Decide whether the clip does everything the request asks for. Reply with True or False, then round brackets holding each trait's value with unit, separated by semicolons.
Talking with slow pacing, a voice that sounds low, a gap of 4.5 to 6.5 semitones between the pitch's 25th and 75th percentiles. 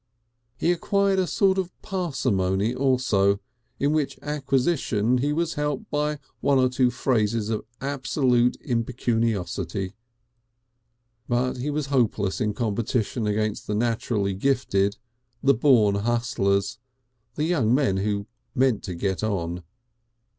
True (125 wpm; 120 Hz; 5.2 semitones)